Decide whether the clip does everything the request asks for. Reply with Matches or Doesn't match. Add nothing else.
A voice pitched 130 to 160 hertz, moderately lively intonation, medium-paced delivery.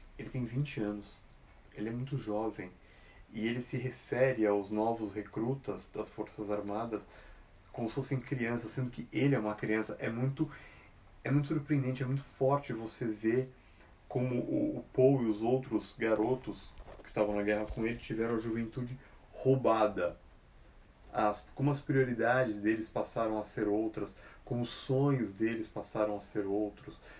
Doesn't match